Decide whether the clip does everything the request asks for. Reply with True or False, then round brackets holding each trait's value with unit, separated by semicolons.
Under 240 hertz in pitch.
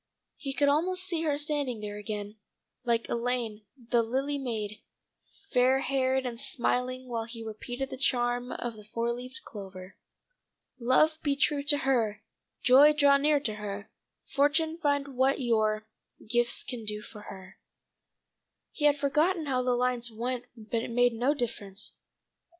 False (250 Hz)